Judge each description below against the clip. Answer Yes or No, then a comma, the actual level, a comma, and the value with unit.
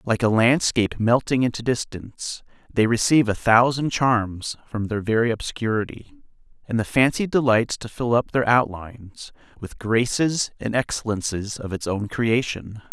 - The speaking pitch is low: Yes, low, 115 Hz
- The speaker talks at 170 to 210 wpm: No, average, 150 wpm